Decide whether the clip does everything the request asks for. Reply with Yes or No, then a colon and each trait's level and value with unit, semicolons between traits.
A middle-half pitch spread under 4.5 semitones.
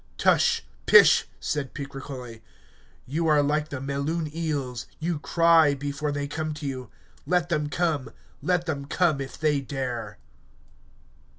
Yes: narrow, 2.4 semitones